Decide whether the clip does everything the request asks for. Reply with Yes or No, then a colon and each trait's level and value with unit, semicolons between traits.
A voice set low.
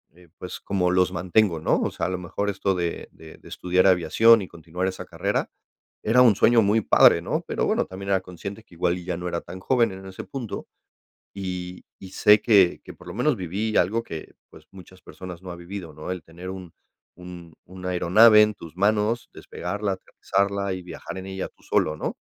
Yes: very low, 95 Hz